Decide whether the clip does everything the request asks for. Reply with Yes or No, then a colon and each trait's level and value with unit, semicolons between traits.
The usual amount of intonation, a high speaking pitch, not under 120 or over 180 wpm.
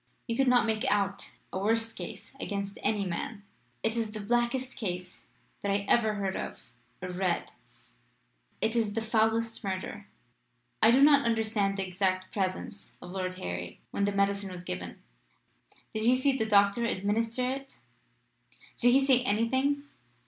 Yes: average, 3.1 semitones; high, 215 Hz; average, 160 wpm